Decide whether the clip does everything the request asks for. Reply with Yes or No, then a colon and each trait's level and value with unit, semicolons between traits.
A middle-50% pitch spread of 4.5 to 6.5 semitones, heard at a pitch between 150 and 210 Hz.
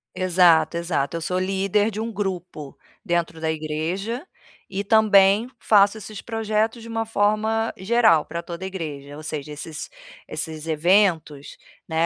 Yes: average, 4.9 semitones; medium, 185 Hz